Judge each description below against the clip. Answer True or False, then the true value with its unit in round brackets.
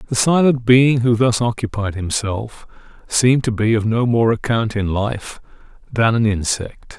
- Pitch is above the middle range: False (115 Hz)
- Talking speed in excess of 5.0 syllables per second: False (4.3 syllables/s)